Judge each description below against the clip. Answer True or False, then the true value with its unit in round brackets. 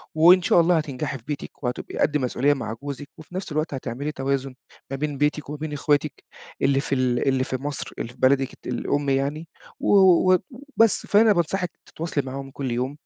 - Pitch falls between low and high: True (145 Hz)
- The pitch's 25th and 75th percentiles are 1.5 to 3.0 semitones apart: True (2.7 semitones)